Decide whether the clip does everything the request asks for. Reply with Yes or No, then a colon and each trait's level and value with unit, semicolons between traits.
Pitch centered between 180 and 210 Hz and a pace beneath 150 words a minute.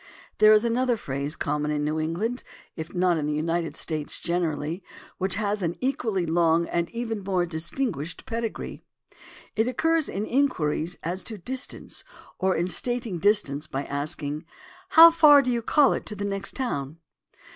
No: medium, 185 Hz; average, 165 wpm